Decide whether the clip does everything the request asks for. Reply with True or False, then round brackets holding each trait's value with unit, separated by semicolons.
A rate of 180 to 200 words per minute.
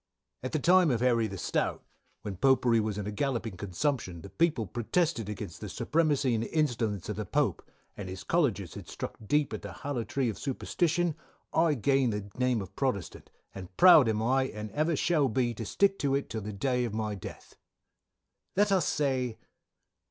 True (195 wpm)